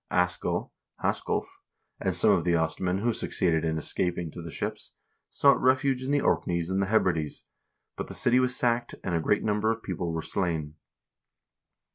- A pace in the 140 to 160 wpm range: No, average, 180 wpm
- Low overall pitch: Yes, very low, 90 Hz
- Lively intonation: Yes, wide, 5.9 semitones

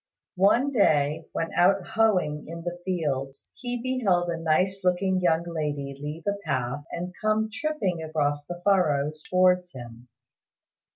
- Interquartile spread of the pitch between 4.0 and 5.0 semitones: Yes, average, 4.5 semitones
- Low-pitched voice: No, medium, 175 Hz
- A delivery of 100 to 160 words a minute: Yes, average, 140 wpm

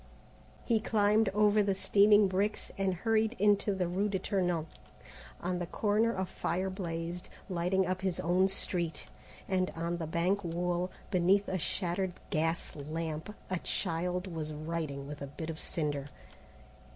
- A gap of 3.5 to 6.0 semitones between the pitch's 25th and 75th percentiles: No, average, 3.0 semitones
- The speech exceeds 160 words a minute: No, average, 150 wpm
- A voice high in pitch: No, medium, 180 Hz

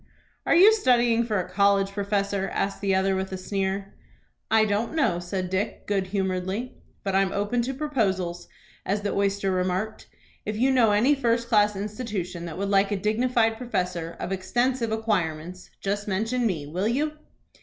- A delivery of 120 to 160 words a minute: No, average, 170 wpm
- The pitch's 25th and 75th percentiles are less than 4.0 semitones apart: Yes, average, 3.3 semitones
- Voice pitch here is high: Yes, high, 200 Hz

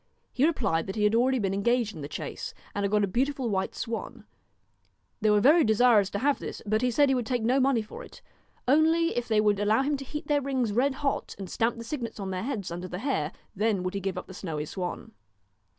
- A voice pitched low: No, high, 225 Hz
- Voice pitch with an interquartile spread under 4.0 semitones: No, average, 4.9 semitones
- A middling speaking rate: No, fast, 255 wpm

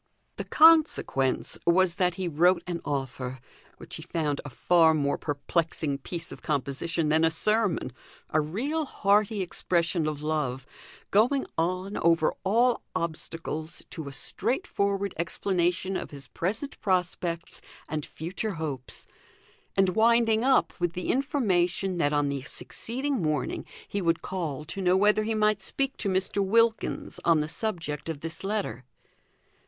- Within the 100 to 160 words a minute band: Yes, average, 145 wpm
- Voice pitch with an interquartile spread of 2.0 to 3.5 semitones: No, average, 4.7 semitones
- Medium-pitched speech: Yes, medium, 175 Hz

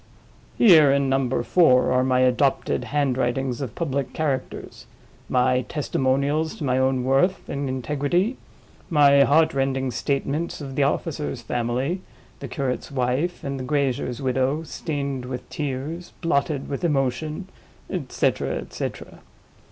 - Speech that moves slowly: Yes, slow, 130 wpm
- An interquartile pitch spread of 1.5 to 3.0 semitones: Yes, narrow, 2.5 semitones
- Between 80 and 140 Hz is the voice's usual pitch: Yes, low, 135 Hz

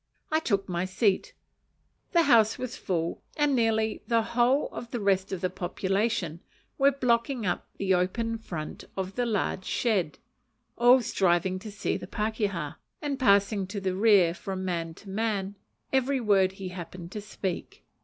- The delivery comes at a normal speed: Yes, average, 165 wpm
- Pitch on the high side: Yes, high, 200 Hz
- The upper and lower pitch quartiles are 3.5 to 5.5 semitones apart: Yes, average, 3.9 semitones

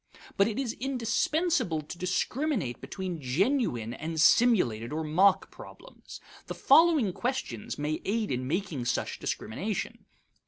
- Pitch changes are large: Yes, wide, 8.5 semitones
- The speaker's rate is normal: No, slow, 125 wpm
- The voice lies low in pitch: No, medium, 185 Hz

